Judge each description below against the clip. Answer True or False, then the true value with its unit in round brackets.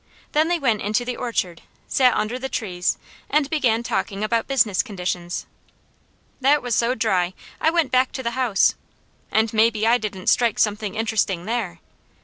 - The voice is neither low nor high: False (225 Hz)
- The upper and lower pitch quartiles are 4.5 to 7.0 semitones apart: False (3.7 semitones)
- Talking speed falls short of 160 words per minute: False (165 wpm)